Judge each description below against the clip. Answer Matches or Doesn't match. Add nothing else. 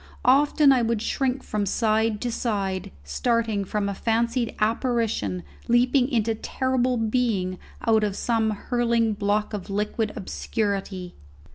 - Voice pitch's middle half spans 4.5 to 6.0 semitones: Doesn't match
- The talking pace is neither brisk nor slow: Doesn't match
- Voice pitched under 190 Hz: Doesn't match